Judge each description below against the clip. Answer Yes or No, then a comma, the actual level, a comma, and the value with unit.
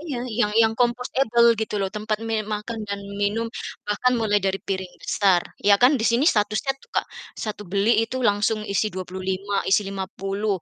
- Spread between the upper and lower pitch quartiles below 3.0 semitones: Yes, narrow, 2.5 semitones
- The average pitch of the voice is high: Yes, high, 210 Hz